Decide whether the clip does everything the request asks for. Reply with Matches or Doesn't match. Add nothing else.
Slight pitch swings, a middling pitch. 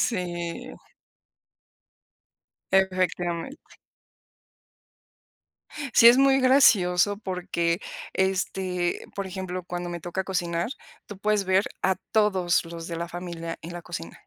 Matches